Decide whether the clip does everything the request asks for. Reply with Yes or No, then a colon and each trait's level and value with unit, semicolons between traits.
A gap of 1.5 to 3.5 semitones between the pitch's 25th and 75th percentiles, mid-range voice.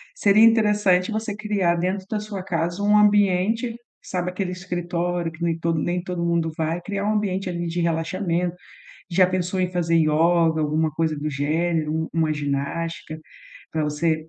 Yes: average, 2.9 semitones; medium, 175 Hz